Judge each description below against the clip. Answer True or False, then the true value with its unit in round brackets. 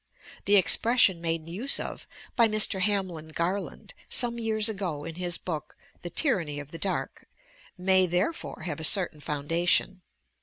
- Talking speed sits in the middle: True (150 wpm)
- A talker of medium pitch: True (180 Hz)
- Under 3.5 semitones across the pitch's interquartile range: False (3.8 semitones)